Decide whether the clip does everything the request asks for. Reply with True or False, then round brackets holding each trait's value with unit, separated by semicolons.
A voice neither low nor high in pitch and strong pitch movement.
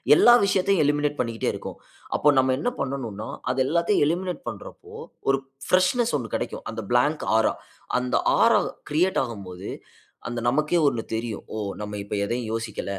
False (130 Hz; 6.6 semitones)